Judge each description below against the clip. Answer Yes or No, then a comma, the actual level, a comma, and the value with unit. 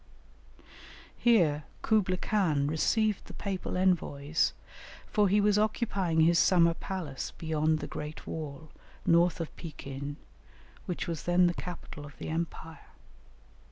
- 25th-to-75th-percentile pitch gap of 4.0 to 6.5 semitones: No, average, 3.4 semitones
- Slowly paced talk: Yes, slow, 125 wpm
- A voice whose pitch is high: No, medium, 170 Hz